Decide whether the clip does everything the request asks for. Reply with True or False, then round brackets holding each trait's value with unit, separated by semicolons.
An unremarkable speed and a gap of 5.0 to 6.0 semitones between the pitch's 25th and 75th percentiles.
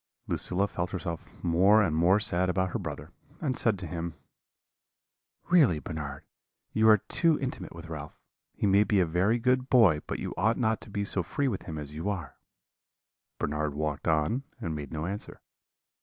True (185 wpm; 5.4 semitones)